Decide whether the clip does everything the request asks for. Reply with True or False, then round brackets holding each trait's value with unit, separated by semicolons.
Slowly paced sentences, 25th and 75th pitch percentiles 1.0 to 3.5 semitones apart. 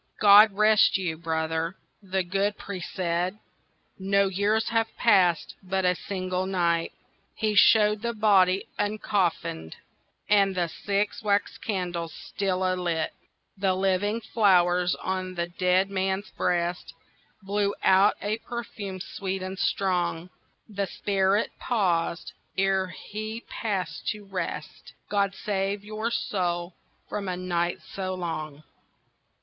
True (120 wpm; 2.4 semitones)